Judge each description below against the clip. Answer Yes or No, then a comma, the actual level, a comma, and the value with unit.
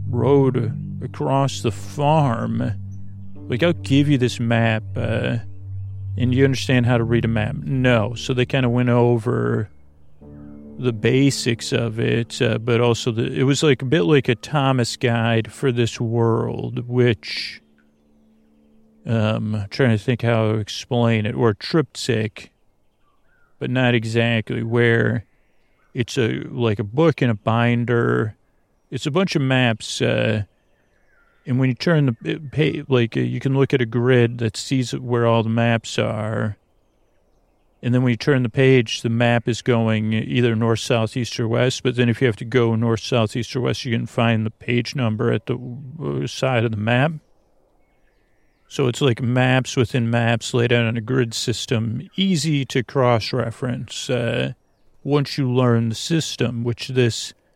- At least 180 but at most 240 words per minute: No, average, 170 wpm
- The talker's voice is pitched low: Yes, low, 120 Hz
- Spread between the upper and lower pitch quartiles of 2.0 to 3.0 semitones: Yes, narrow, 2.4 semitones